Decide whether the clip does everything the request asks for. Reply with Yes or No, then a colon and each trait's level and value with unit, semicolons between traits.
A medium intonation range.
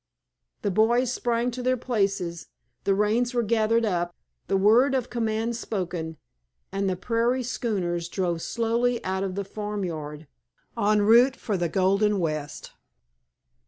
Yes: average, 4.2 semitones